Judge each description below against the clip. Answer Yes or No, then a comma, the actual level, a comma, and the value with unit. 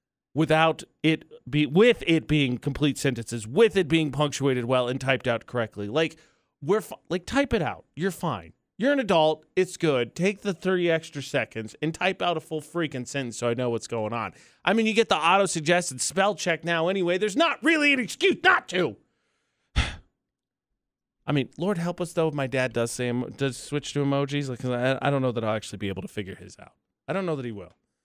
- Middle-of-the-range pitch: Yes, medium, 155 Hz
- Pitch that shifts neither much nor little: No, wide, 6.0 semitones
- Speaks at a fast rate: Yes, fast, 220 wpm